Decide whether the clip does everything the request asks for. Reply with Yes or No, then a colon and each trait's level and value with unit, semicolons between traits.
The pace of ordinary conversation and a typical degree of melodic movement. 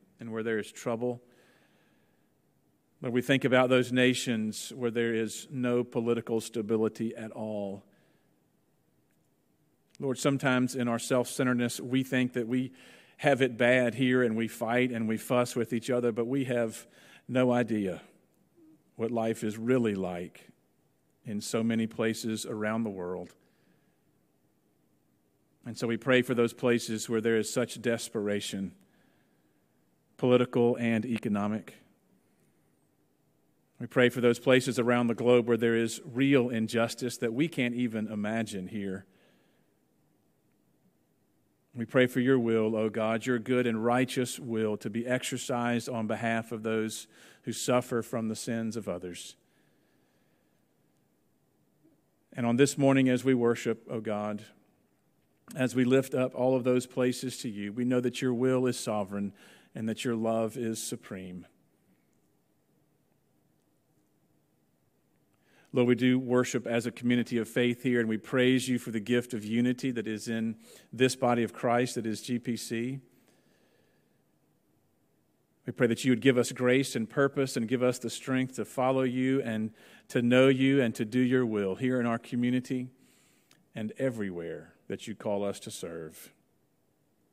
No: average, 150 wpm; narrow, 2.2 semitones